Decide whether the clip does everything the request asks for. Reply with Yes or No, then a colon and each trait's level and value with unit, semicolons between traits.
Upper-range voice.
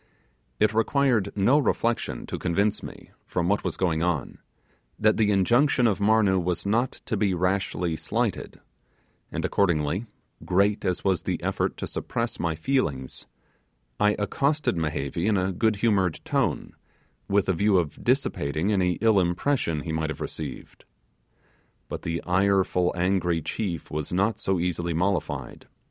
No: very low, 95 Hz